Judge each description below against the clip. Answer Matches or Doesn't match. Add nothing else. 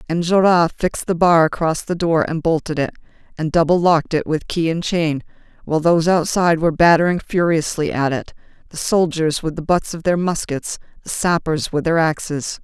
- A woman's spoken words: Matches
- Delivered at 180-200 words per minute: Matches